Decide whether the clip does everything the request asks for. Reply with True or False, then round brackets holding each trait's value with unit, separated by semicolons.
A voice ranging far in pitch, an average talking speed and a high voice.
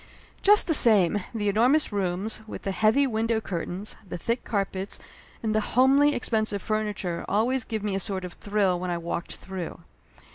False (3.2 semitones; 175 wpm; 210 Hz)